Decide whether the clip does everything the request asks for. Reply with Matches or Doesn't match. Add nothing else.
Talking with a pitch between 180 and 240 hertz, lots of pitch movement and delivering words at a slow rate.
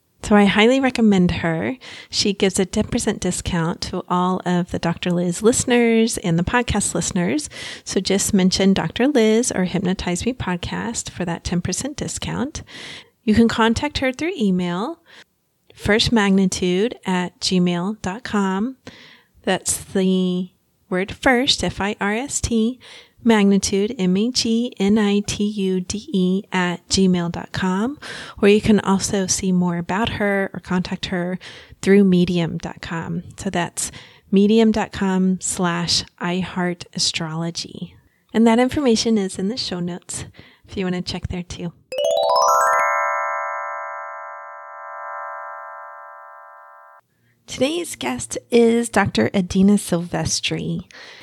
Doesn't match